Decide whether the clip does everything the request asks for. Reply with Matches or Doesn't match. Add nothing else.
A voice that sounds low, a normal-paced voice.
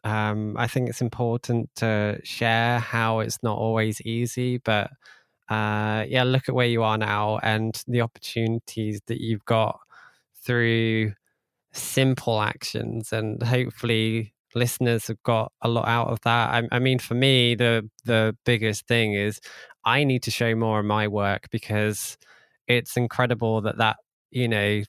Matches